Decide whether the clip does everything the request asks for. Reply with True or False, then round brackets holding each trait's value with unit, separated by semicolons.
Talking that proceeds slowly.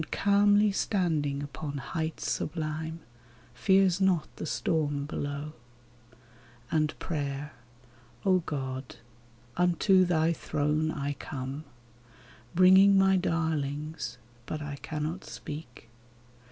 True (100 wpm)